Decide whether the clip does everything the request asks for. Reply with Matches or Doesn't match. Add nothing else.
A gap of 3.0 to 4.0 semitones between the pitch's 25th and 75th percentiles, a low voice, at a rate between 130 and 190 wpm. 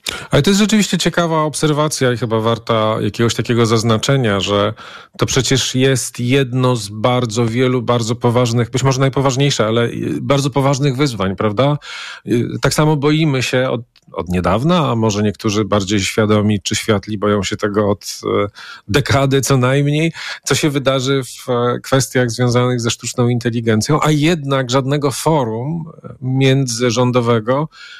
Matches